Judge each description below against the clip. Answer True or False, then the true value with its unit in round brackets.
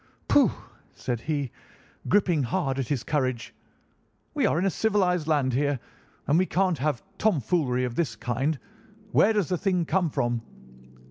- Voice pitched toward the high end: False (150 Hz)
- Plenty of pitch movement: True (5.9 semitones)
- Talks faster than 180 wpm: False (155 wpm)